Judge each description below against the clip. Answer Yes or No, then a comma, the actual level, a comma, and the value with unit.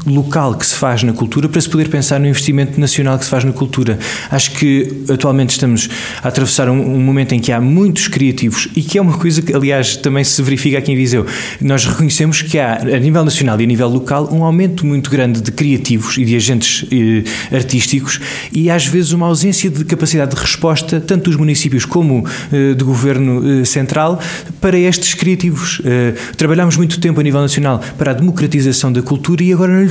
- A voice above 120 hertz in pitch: Yes, medium, 140 Hz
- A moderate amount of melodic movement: Yes, average, 3.7 semitones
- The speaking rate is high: Yes, fast, 205 wpm